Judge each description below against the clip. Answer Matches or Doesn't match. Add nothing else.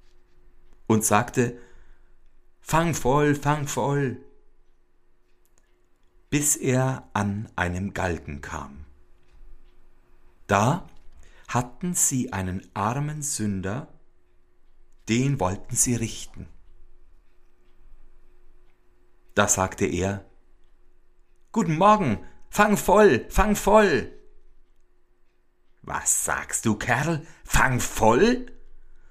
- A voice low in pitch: Matches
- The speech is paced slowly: Matches